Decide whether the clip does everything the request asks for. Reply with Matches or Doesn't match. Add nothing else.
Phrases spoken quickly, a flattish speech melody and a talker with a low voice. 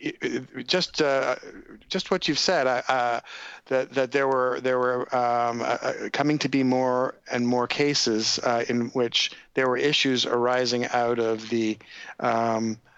Doesn't match